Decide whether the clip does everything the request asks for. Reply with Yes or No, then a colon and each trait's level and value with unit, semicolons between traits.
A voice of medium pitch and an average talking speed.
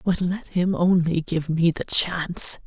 Yes: medium, 175 Hz; average, 180 wpm